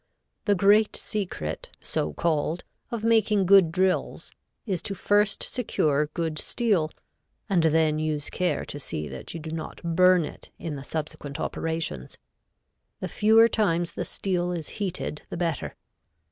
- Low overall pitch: No, medium, 170 Hz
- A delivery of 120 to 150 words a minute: Yes, average, 145 wpm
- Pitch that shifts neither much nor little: Yes, average, 4.3 semitones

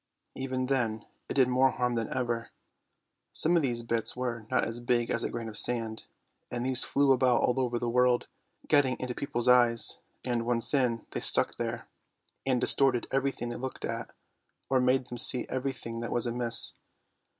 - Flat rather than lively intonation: Yes, narrow, 1.8 semitones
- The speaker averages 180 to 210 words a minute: Yes, average, 185 wpm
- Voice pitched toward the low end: Yes, low, 125 Hz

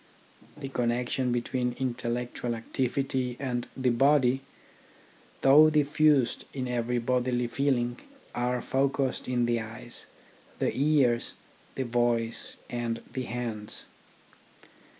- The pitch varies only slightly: Yes, narrow, 1.9 semitones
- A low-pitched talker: Yes, low, 125 Hz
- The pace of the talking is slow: Yes, slow, 105 wpm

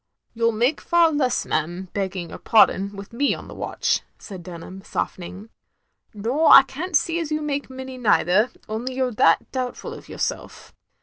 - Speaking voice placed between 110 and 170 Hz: No, high, 235 Hz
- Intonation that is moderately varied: No, wide, 6.0 semitones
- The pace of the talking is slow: No, average, 180 wpm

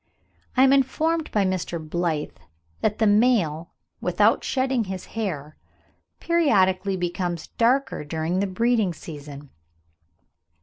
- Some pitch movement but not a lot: No, wide, 6.3 semitones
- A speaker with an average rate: No, slow, 115 wpm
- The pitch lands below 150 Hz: No, high, 190 Hz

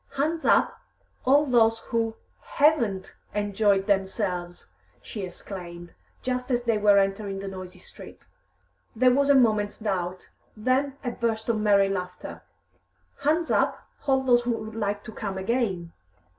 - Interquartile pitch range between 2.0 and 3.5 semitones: No, average, 4.3 semitones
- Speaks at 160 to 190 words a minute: No, average, 145 wpm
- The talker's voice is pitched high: Yes, high, 215 Hz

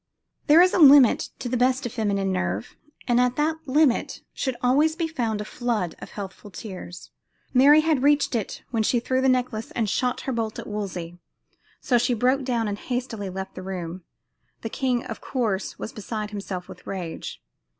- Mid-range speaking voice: No, high, 235 Hz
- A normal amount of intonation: Yes, average, 4.4 semitones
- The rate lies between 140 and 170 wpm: No, average, 190 wpm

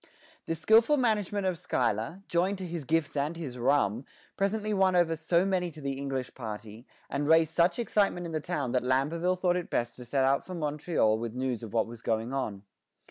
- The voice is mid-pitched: Yes, medium, 155 Hz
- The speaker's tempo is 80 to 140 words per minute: No, fast, 205 wpm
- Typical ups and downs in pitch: No, wide, 6.0 semitones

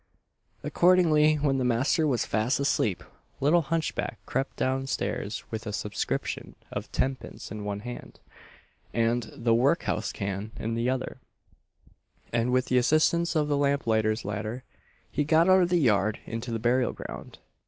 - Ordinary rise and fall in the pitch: Yes, average, 5.0 semitones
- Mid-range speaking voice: No, low, 125 Hz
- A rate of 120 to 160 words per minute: Yes, average, 155 wpm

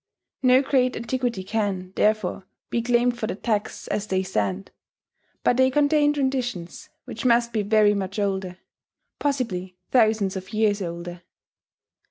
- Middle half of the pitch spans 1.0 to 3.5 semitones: No, average, 4.7 semitones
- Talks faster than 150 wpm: No, average, 140 wpm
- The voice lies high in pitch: Yes, high, 215 Hz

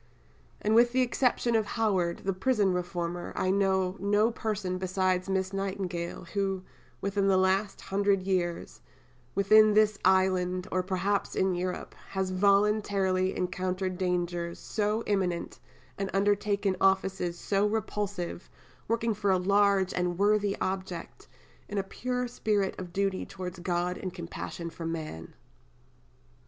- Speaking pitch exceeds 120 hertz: Yes, high, 190 Hz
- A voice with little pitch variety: Yes, narrow, 2.0 semitones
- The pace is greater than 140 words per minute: No, slow, 135 wpm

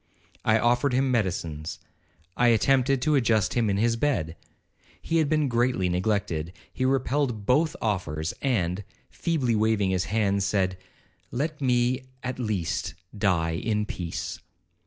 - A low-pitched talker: Yes, low, 110 Hz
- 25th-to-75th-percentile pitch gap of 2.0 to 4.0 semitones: No, wide, 5.5 semitones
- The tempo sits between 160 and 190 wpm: No, slow, 135 wpm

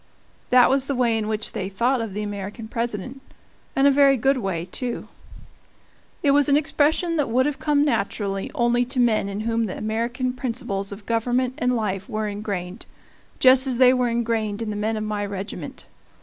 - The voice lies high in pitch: Yes, high, 230 Hz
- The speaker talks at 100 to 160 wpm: No, average, 190 wpm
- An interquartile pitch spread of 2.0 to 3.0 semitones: No, average, 3.6 semitones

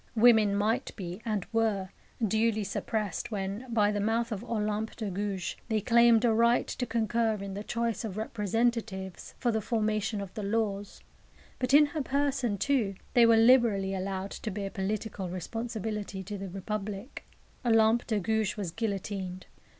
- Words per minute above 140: Yes, average, 160 wpm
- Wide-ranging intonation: No, average, 2.7 semitones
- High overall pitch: Yes, high, 215 Hz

